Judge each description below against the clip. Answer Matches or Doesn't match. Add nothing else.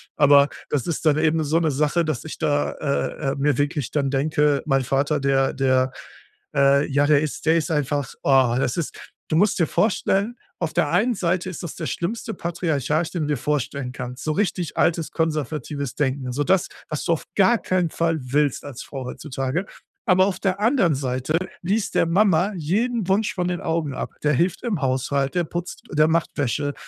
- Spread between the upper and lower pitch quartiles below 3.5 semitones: Doesn't match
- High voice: Doesn't match